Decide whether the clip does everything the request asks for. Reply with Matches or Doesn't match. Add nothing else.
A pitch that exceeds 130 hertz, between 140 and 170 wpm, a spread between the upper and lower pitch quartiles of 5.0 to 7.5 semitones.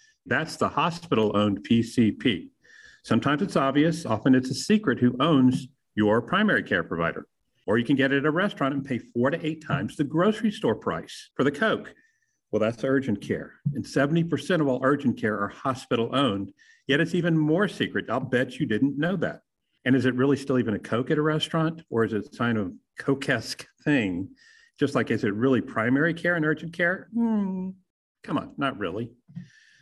Doesn't match